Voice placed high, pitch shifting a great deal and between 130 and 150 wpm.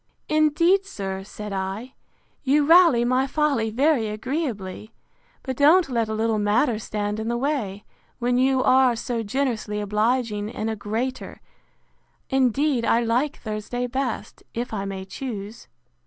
No: high, 235 Hz; average, 4.1 semitones; average, 140 wpm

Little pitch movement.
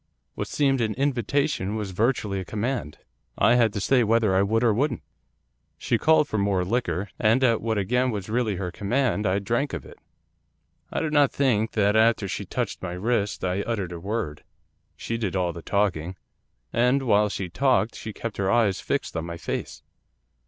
No: average, 3.8 semitones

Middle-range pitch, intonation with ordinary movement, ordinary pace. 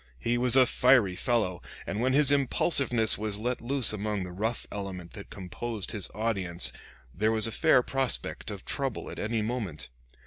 No: low, 110 Hz; average, 3.9 semitones; average, 175 wpm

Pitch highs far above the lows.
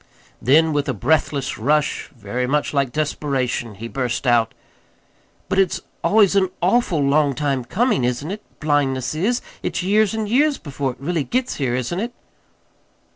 Yes: wide, 6.7 semitones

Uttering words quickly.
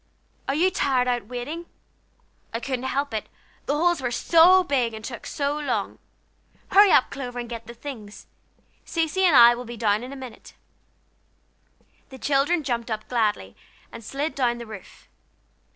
No: average, 170 wpm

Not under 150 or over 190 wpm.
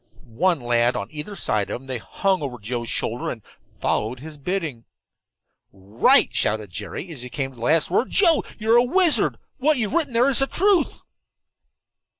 Yes: average, 185 wpm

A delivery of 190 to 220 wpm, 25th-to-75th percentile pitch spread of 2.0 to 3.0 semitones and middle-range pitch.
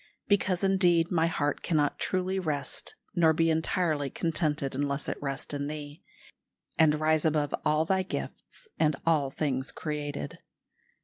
No: average, 140 wpm; narrow, 2.5 semitones; medium, 155 Hz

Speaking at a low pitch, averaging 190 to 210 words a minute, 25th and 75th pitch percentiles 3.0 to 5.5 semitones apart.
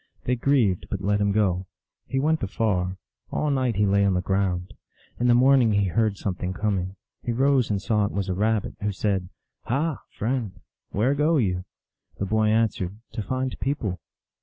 Yes: low, 105 Hz; average, 195 wpm; average, 4.4 semitones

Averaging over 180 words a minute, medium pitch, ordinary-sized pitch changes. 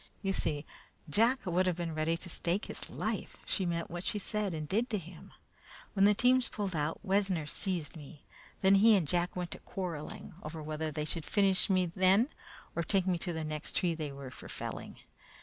Yes: fast, 205 wpm; medium, 175 Hz; average, 3.7 semitones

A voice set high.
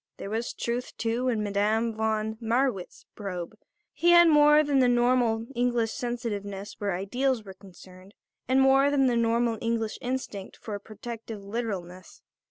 Yes: high, 230 Hz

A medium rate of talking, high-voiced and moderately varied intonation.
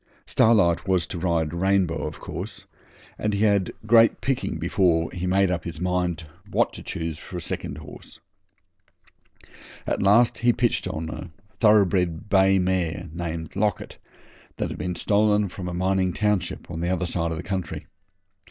No: average, 160 wpm; very low, 90 Hz; average, 3.0 semitones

